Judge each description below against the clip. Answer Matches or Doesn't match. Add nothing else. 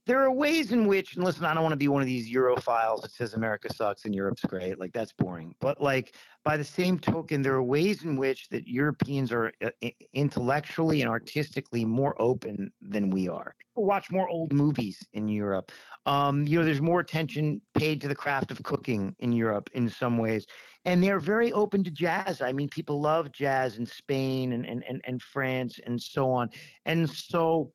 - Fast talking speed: Matches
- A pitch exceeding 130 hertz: Matches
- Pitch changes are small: Doesn't match